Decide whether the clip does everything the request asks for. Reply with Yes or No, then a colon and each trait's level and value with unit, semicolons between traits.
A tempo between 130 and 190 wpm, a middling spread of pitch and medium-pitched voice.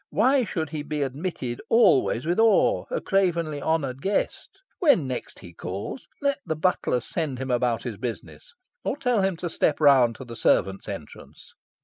No: average, 170 wpm; wide, 7.5 semitones; medium, 155 Hz